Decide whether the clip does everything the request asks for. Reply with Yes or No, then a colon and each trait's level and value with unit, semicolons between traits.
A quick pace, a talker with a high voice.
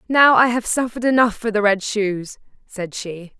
No: average, 195 wpm; high, 220 Hz